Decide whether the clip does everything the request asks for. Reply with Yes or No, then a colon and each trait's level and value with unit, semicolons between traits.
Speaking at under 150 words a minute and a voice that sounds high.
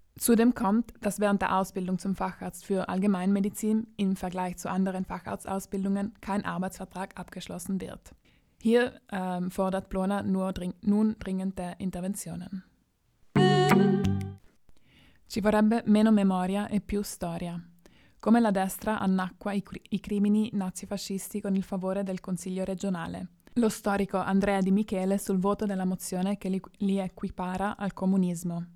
Yes: average, 135 wpm; high, 195 Hz